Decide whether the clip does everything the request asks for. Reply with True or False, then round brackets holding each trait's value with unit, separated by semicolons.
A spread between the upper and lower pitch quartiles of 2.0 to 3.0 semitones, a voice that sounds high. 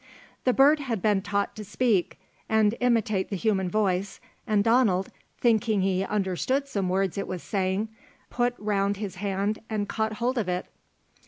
True (2.7 semitones; 205 Hz)